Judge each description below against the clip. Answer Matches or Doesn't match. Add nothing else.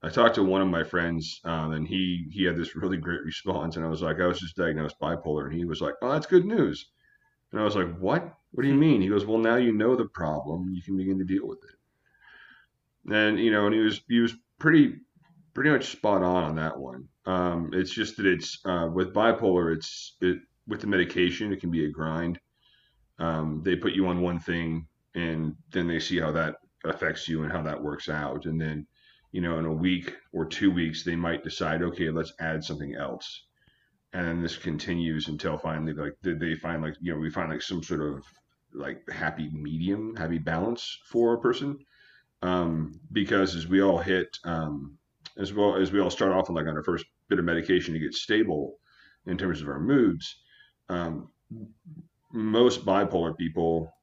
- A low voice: Matches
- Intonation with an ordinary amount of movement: Matches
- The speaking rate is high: Matches